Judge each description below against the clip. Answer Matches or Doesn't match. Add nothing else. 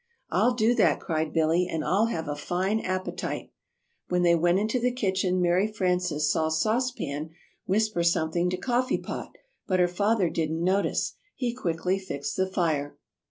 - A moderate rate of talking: Matches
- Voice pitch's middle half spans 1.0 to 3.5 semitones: Doesn't match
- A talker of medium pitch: Matches